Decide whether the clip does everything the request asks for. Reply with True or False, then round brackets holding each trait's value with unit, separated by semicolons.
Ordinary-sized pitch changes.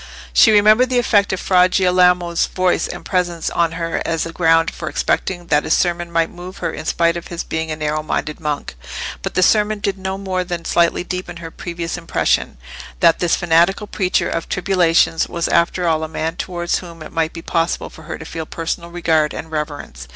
False (1.9 semitones)